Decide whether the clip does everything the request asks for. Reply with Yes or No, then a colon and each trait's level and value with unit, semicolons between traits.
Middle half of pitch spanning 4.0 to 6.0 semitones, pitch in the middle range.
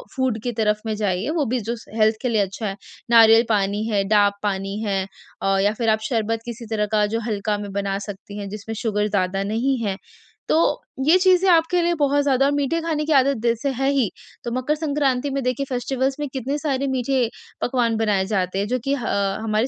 No: average, 4.7 semitones; high, 230 Hz